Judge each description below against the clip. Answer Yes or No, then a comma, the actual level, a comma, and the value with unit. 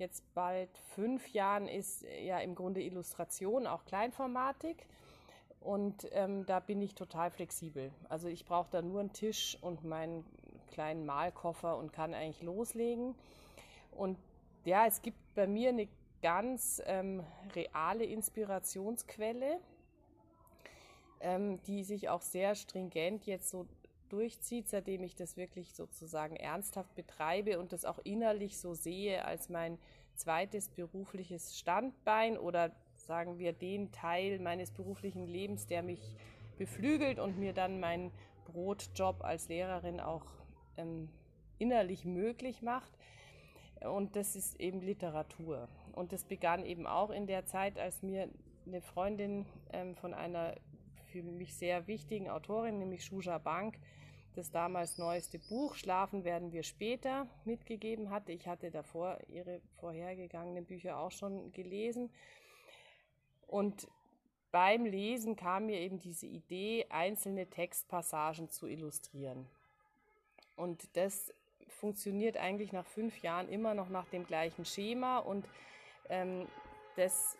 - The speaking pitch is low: No, medium, 185 Hz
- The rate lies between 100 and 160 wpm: Yes, average, 130 wpm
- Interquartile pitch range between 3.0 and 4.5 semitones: Yes, average, 3.3 semitones